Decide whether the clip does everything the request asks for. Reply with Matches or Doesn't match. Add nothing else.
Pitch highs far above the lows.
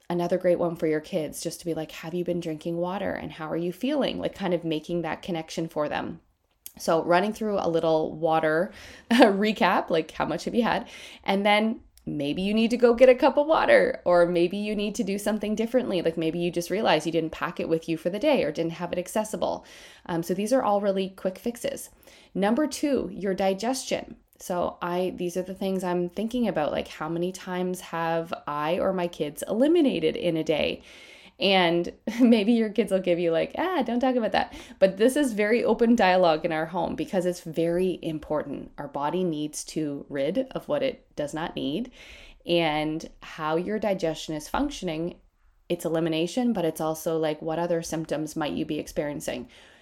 Doesn't match